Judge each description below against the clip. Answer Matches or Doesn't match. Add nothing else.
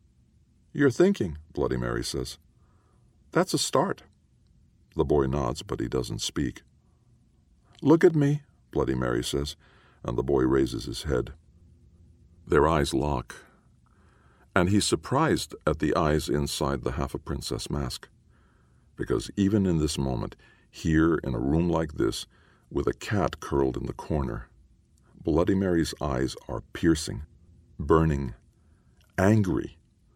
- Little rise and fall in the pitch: Doesn't match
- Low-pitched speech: Matches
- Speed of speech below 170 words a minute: Matches